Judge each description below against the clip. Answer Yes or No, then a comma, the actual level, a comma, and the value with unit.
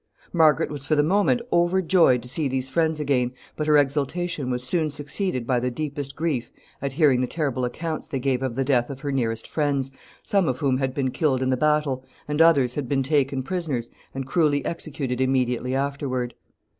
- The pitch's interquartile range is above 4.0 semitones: No, average, 3.1 semitones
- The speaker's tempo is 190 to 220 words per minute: Yes, average, 195 wpm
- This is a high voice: No, medium, 140 Hz